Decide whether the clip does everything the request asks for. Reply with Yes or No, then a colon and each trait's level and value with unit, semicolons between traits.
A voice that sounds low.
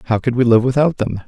Yes: low, 125 Hz